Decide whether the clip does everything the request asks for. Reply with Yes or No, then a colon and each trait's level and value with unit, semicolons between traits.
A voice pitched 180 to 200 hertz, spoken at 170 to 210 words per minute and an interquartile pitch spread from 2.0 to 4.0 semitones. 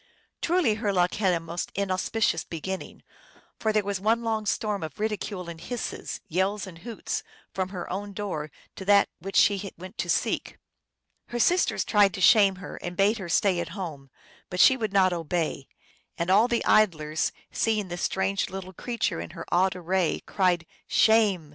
Yes: high, 190 Hz; average, 180 wpm; average, 3.2 semitones